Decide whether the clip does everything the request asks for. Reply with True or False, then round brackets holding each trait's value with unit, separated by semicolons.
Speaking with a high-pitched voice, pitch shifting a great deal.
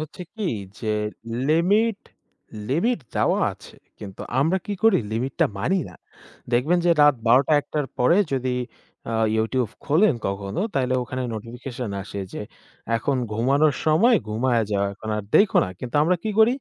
False (135 Hz; 7.1 semitones)